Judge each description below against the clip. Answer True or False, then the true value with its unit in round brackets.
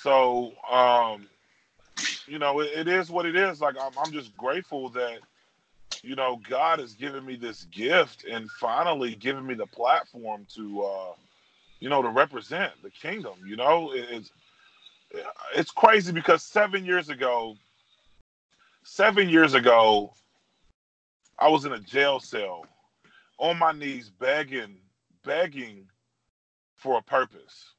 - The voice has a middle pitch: False (130 Hz)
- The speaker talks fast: False (140 wpm)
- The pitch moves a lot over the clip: True (6.3 semitones)